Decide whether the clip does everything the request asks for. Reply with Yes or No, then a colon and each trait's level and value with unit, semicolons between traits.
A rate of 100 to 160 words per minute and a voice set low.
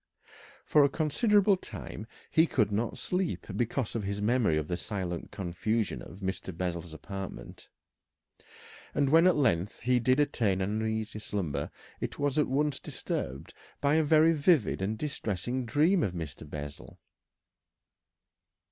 Yes: average, 145 wpm; low, 110 Hz